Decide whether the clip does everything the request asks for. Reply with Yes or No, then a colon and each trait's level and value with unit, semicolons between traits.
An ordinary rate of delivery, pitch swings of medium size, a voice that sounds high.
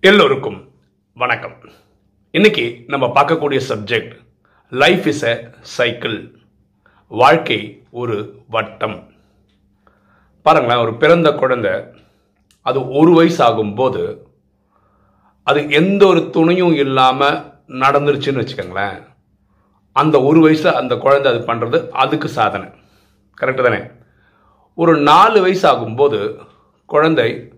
No: average, 95 wpm; average, 4.3 semitones; medium, 150 Hz